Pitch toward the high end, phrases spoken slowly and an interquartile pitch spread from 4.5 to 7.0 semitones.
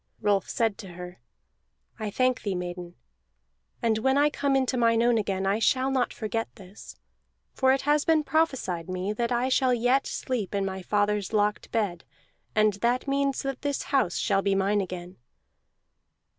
No: high, 220 Hz; average, 170 wpm; average, 5.1 semitones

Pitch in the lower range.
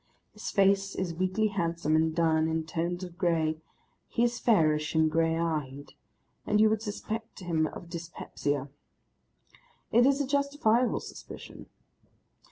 No: medium, 170 Hz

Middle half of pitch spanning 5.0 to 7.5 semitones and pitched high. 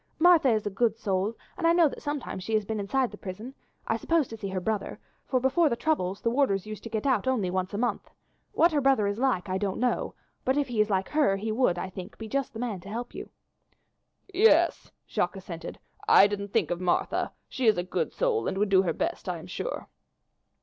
Yes: wide, 5.5 semitones; high, 220 Hz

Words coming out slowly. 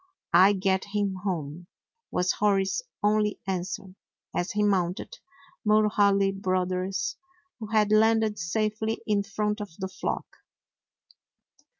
Yes: slow, 110 wpm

